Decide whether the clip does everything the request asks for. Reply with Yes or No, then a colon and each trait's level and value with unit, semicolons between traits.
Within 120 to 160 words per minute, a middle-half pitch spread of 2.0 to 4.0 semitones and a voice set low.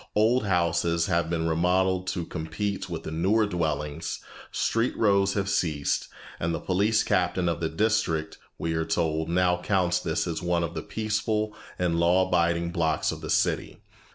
No: average, 170 wpm; average, 2.9 semitones; very low, 85 Hz